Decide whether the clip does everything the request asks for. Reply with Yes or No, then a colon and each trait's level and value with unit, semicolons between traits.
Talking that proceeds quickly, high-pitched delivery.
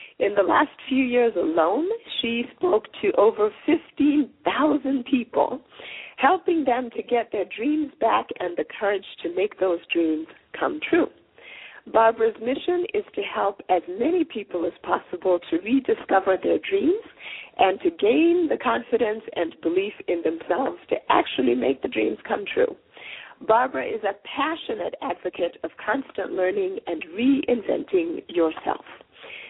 No: average, 140 wpm; very high, 260 Hz